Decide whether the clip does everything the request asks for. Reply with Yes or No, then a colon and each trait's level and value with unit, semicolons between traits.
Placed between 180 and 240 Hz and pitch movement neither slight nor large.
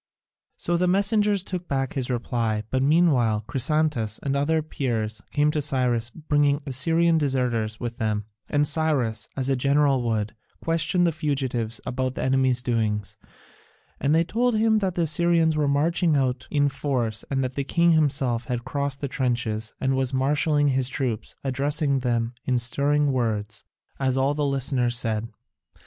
No: low, 135 Hz; average, 3.9 semitones